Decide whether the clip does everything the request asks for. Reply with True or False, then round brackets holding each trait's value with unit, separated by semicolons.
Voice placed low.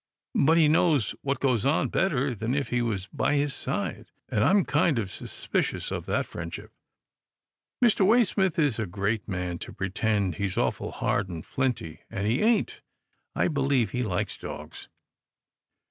True (125 Hz)